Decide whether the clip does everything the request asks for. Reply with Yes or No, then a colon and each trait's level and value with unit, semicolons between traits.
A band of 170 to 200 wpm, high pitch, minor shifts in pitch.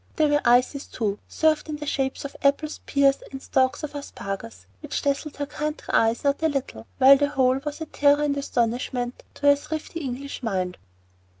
No: average, 190 wpm; very high, 280 Hz; average, 3.0 semitones